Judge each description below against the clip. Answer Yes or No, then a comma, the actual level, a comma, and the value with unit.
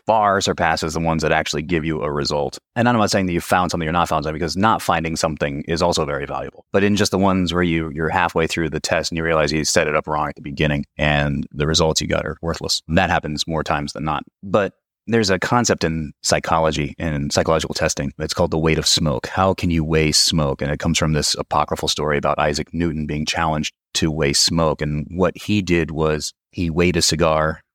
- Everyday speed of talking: No, fast, 240 wpm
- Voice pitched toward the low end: Yes, very low, 80 Hz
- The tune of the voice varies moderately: No, narrow, 2.2 semitones